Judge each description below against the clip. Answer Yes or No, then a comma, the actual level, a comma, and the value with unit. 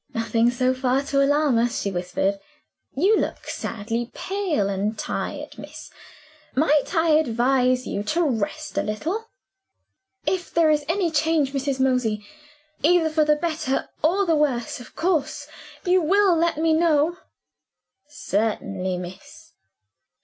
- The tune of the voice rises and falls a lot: Yes, wide, 5.8 semitones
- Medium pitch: No, very high, 285 Hz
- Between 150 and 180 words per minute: No, slow, 135 wpm